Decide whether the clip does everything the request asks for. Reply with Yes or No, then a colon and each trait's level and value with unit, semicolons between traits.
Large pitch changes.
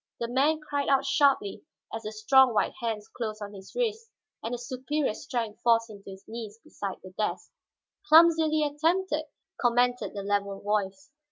Yes: wide, 5.7 semitones